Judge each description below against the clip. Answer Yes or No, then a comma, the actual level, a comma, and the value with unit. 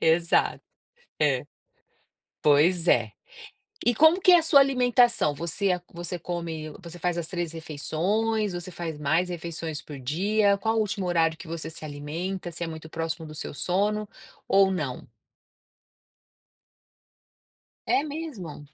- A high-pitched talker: No, medium, 175 Hz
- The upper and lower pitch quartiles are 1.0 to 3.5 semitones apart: No, average, 4.2 semitones